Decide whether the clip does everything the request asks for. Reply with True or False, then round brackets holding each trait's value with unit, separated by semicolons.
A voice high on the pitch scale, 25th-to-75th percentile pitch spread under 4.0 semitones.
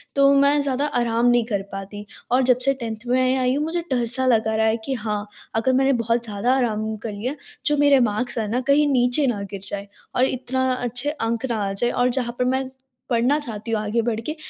True (245 Hz; 2.9 semitones)